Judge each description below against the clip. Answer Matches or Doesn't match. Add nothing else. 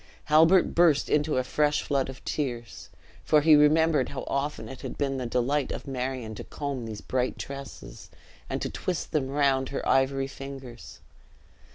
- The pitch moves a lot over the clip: Doesn't match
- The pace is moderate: Matches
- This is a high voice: Doesn't match